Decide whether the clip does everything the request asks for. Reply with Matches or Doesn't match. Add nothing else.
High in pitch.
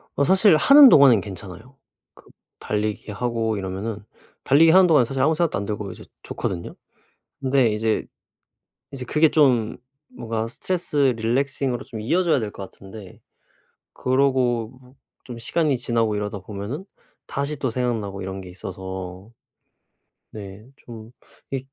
Doesn't match